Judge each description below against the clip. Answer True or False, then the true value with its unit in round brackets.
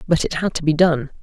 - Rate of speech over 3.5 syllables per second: True (6.1 syllables/s)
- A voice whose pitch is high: False (160 Hz)